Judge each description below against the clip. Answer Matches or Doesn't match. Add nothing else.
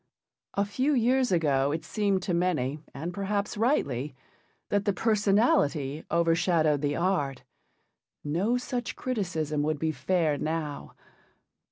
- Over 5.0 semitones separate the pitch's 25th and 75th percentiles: Matches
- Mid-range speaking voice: Matches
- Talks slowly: Matches